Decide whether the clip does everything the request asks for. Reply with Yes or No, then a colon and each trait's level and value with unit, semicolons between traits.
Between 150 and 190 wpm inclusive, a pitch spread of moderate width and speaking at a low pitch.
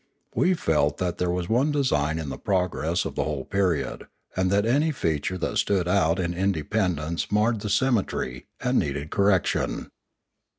Yes: average, 165 wpm; average, 4.6 semitones; very low, 90 Hz